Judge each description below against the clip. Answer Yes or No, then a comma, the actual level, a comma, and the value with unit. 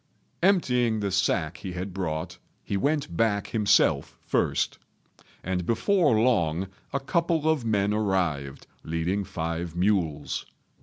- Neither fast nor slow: No, slow, 120 wpm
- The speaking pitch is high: No, low, 100 Hz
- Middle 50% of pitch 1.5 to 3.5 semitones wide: No, wide, 5.6 semitones